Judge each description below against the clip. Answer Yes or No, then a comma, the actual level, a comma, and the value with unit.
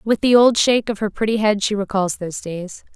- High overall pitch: Yes, high, 210 Hz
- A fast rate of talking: Yes, fast, 245 wpm